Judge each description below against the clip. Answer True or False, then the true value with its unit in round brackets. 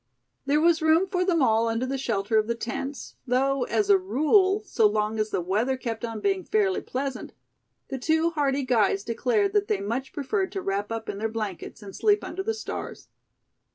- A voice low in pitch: False (265 Hz)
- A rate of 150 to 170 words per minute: False (200 wpm)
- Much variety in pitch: True (8.3 semitones)